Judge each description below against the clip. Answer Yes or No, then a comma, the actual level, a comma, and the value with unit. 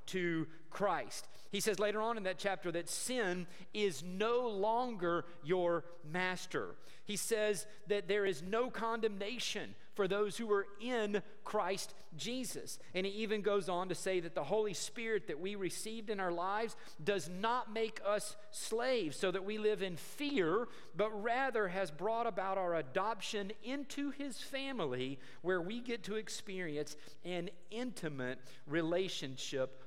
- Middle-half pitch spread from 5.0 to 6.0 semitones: No, average, 3.8 semitones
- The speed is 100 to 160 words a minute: Yes, average, 155 wpm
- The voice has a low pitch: No, high, 200 Hz